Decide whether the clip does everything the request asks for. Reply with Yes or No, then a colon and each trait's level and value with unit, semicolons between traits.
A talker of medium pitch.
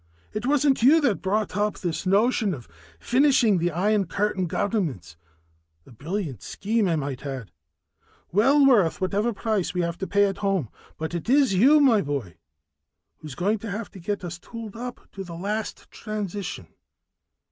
No: high, 200 Hz